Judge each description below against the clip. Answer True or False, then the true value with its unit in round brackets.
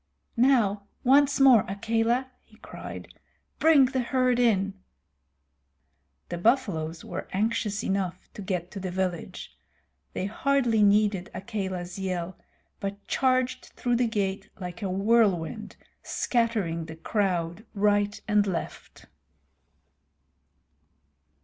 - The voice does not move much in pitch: False (4.0 semitones)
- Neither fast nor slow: False (110 wpm)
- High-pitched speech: True (205 Hz)